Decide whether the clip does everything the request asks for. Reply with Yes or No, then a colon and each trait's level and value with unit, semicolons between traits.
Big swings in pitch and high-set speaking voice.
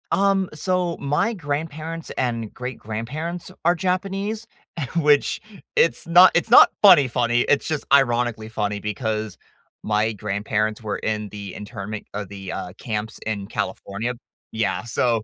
No: wide, 7.5 semitones; low, 120 Hz